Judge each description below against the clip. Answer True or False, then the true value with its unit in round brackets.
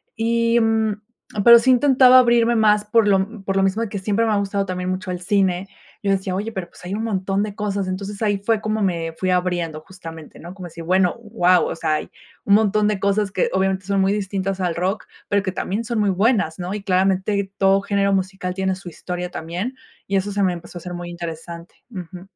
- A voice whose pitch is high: True (195 Hz)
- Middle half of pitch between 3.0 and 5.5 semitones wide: False (2.5 semitones)